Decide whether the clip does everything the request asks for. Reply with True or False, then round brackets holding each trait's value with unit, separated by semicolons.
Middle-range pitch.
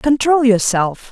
False (240 Hz)